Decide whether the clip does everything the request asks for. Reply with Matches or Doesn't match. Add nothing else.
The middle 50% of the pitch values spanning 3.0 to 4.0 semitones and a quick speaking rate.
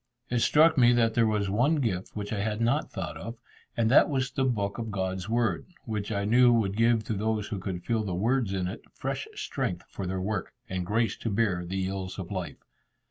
Matches